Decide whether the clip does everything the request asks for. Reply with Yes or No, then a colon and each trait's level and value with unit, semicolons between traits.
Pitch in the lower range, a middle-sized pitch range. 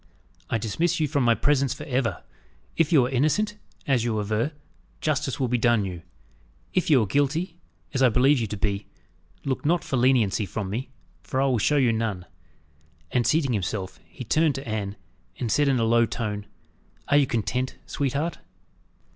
Yes: low, 125 Hz; average, 4.5 semitones